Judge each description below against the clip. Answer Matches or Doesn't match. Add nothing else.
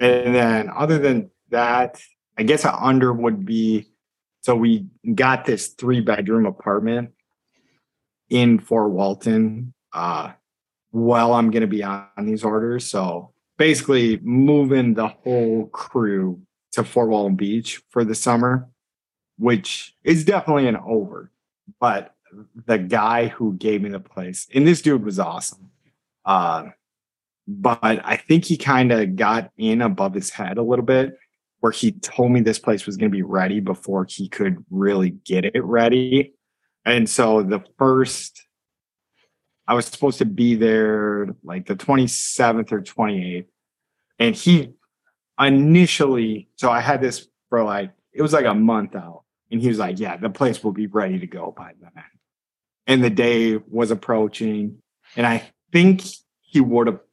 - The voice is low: Matches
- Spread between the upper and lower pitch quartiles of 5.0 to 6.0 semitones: Doesn't match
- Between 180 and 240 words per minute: Doesn't match